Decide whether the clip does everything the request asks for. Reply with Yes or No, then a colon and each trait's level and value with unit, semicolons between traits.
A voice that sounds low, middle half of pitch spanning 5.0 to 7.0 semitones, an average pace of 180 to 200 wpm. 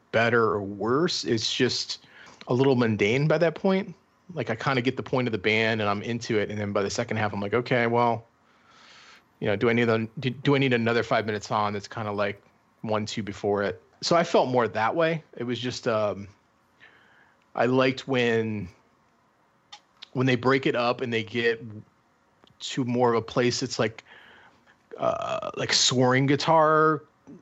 No: low, 120 Hz; average, 3.3 semitones; average, 195 wpm